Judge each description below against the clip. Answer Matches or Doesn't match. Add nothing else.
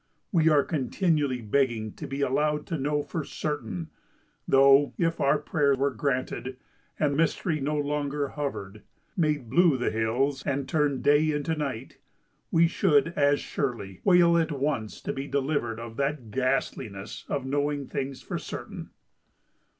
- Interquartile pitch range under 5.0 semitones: Matches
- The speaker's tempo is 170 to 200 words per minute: Doesn't match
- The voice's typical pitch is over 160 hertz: Doesn't match